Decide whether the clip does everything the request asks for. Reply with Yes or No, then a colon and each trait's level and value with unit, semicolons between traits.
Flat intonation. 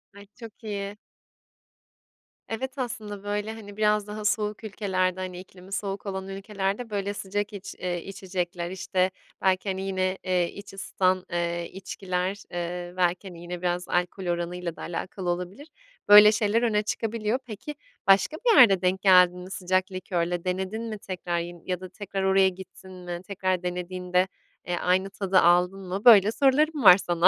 Yes: narrow, 2.3 semitones